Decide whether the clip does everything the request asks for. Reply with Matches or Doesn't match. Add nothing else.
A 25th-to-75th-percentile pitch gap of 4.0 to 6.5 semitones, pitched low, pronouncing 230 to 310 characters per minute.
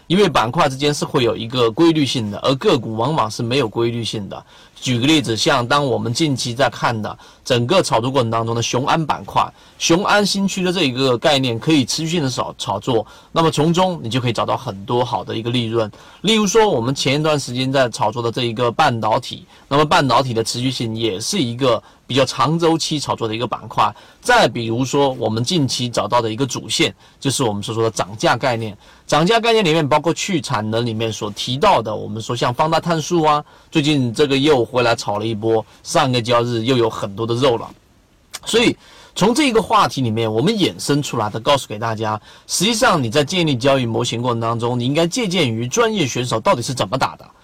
Doesn't match